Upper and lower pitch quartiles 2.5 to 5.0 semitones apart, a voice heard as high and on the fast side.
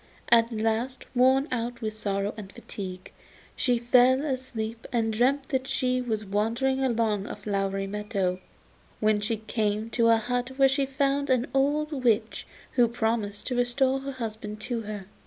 No: average, 3.4 semitones; high, 230 Hz; average, 160 wpm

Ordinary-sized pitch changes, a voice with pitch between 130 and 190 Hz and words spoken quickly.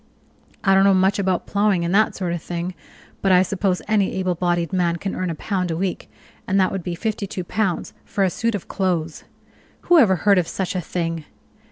No: narrow, 2.2 semitones; medium, 185 Hz; fast, 220 wpm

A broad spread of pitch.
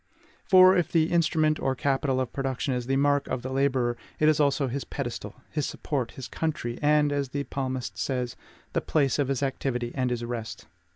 No: average, 2.7 semitones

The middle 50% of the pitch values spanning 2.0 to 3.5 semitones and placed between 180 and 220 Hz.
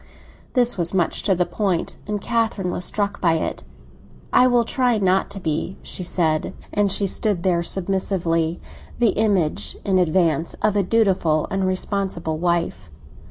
Yes: average, 3.2 semitones; medium, 185 Hz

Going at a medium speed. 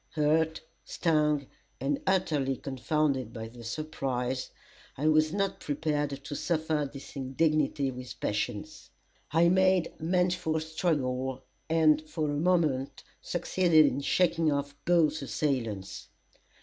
No: slow, 115 wpm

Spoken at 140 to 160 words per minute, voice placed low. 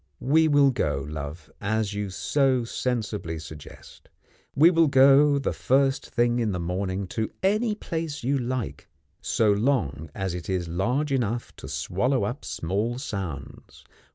Yes: average, 150 wpm; low, 115 Hz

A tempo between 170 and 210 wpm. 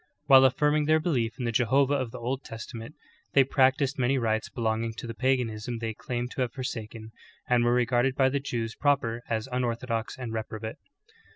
Yes: average, 185 wpm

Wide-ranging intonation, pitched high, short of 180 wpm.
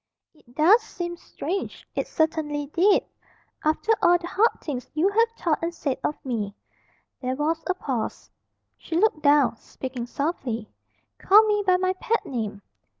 Yes: wide, 5.9 semitones; very high, 315 Hz; average, 155 wpm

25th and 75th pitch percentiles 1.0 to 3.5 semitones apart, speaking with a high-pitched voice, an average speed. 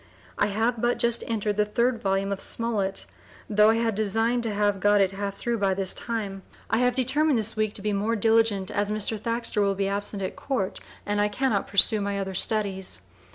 No: narrow, 2.5 semitones; high, 210 Hz; fast, 210 wpm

